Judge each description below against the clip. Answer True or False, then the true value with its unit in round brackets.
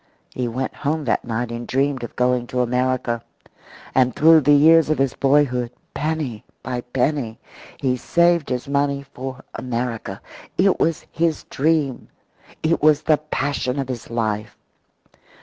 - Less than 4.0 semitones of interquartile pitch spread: True (3.4 semitones)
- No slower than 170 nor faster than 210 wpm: False (150 wpm)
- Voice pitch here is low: True (130 Hz)